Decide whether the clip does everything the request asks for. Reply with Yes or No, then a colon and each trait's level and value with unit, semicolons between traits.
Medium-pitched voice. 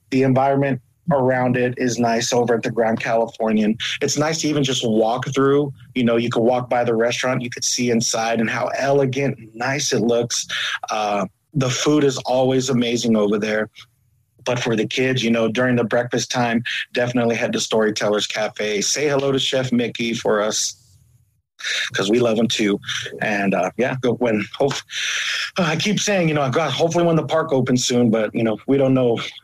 No: low, 120 Hz